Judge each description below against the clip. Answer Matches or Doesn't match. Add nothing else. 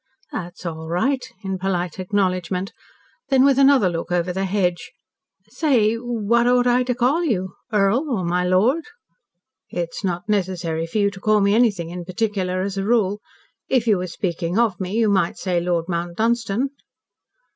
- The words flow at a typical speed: Matches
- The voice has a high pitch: Matches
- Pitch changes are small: Doesn't match